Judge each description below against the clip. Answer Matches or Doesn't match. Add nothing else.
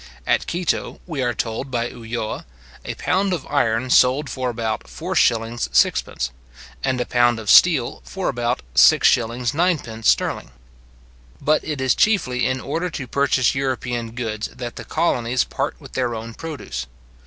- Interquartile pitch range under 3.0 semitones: Doesn't match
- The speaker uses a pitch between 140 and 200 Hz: Doesn't match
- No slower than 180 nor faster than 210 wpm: Doesn't match